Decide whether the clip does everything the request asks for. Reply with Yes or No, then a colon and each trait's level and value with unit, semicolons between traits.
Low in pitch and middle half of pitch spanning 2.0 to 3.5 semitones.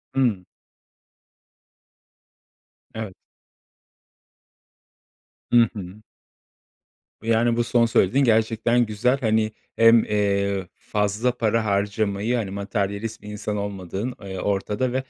Yes: low, 110 Hz; narrow, 2.5 semitones